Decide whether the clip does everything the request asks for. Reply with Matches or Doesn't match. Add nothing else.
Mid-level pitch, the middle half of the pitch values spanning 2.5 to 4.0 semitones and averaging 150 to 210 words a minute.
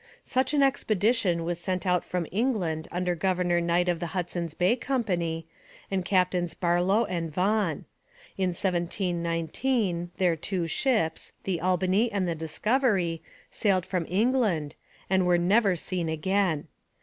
Doesn't match